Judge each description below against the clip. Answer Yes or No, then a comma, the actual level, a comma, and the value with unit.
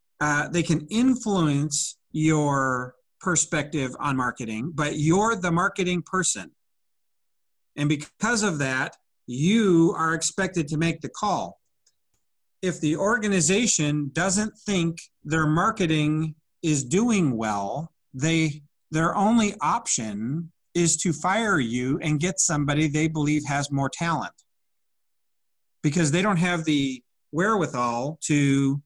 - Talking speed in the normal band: No, slow, 120 wpm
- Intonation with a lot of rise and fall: No, average, 3.6 semitones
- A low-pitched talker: No, medium, 160 Hz